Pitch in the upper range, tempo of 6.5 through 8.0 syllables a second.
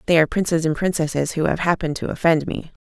No: medium, 165 Hz; 7.0 syllables/s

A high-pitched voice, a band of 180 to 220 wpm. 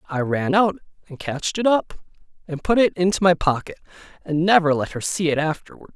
No: medium, 170 Hz; average, 200 wpm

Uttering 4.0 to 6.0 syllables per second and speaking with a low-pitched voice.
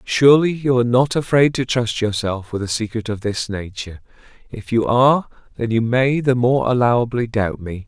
Yes: 5.3 syllables/s; low, 120 Hz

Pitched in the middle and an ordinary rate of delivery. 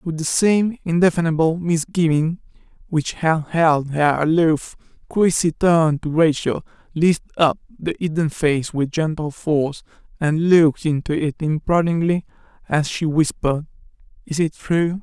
No: medium, 160 Hz; slow, 130 wpm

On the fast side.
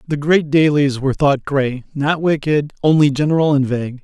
No: average, 165 wpm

